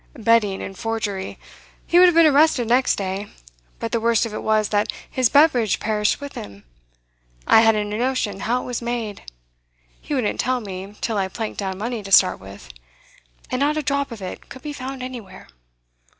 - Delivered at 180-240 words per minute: Yes, average, 195 wpm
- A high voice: Yes, high, 225 Hz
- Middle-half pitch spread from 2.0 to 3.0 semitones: No, average, 4.0 semitones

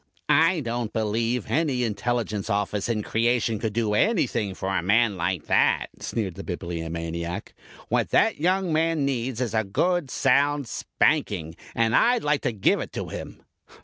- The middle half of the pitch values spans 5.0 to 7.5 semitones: Yes, wide, 5.4 semitones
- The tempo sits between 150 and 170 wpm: Yes, average, 160 wpm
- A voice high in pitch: No, low, 115 Hz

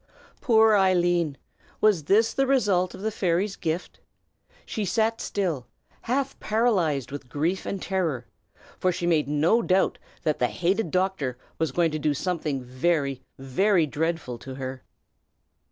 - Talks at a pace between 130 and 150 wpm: Yes, average, 145 wpm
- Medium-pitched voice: Yes, medium, 175 Hz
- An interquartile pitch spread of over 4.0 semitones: Yes, wide, 5.4 semitones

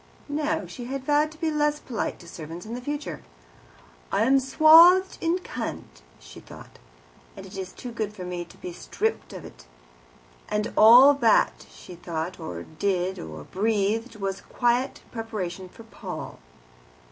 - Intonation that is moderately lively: No, wide, 7.5 semitones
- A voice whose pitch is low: No, high, 225 Hz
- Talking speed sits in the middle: Yes, average, 160 wpm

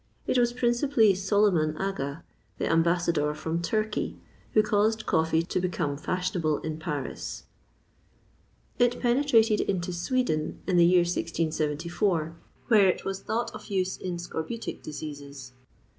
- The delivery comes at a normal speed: No, slow, 130 wpm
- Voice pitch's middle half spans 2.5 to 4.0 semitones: No, average, 5.0 semitones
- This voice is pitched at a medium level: Yes, medium, 180 Hz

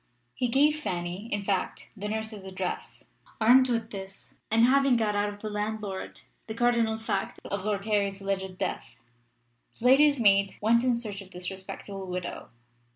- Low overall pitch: No, high, 210 Hz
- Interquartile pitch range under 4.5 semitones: Yes, average, 3.1 semitones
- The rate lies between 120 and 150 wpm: No, average, 165 wpm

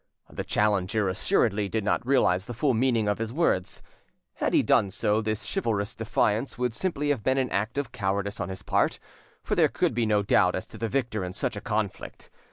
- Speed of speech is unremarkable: No, fast, 210 wpm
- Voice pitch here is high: No, low, 110 Hz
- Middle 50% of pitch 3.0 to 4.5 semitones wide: Yes, average, 3.3 semitones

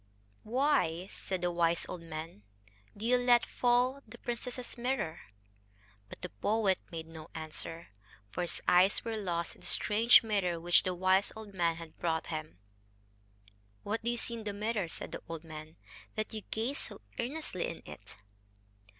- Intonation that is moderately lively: No, wide, 5.7 semitones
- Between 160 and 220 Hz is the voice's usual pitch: Yes, high, 190 Hz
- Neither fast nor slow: Yes, average, 170 wpm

